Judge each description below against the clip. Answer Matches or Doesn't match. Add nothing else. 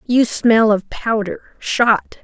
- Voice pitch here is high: Matches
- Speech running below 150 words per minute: Matches